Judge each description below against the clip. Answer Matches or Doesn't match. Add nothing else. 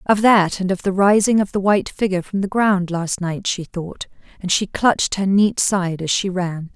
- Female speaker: Matches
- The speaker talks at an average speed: Doesn't match